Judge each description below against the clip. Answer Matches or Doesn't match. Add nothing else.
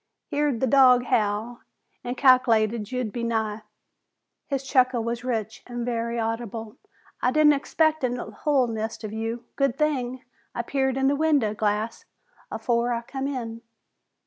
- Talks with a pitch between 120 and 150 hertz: Doesn't match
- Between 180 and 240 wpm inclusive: Doesn't match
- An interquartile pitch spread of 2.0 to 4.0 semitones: Matches